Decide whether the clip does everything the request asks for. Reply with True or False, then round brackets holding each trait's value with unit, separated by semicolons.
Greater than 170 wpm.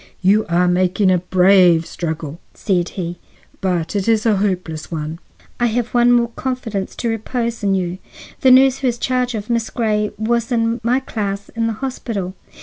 True (180 wpm)